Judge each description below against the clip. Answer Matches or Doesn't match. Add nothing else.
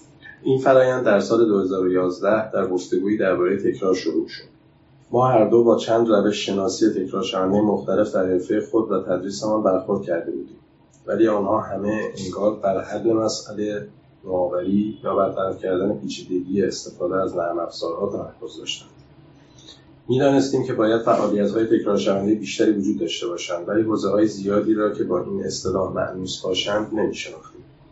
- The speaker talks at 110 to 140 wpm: Doesn't match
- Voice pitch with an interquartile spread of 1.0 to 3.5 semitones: Matches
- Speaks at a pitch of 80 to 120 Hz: Matches